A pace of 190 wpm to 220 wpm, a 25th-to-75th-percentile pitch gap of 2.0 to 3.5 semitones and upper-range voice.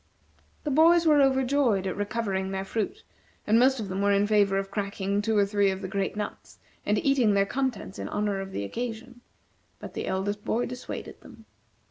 No: average, 195 wpm; average, 4.1 semitones; high, 205 Hz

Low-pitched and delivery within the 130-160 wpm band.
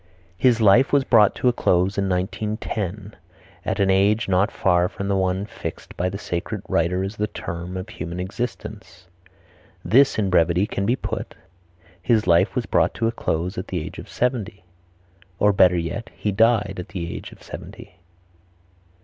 No: low, 100 Hz; average, 175 wpm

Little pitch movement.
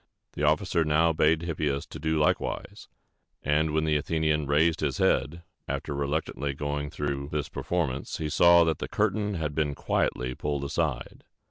Yes: narrow, 2.0 semitones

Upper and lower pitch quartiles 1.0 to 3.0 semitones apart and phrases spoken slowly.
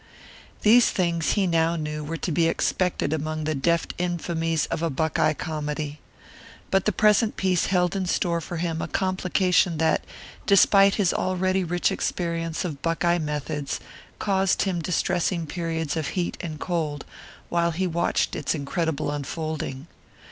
No: narrow, 2.6 semitones; average, 150 wpm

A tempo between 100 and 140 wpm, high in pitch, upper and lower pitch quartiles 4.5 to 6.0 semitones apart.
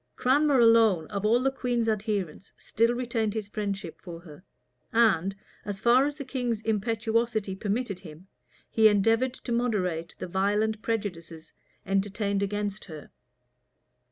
No: slow, 135 wpm; high, 215 Hz; average, 3.2 semitones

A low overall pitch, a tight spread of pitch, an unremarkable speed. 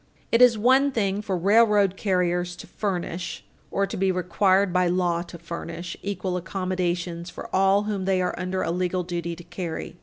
No: medium, 185 Hz; narrow, 2.2 semitones; average, 180 wpm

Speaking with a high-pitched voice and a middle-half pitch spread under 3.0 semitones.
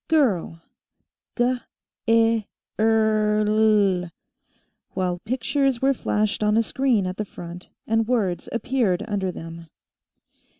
No: high, 215 Hz; average, 3.8 semitones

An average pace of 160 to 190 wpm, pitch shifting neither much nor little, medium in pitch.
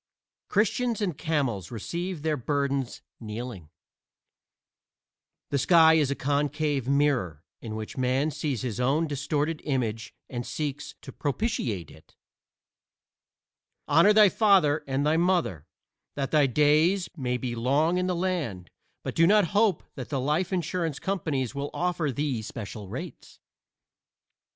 No: slow, 135 wpm; average, 4.9 semitones; medium, 145 Hz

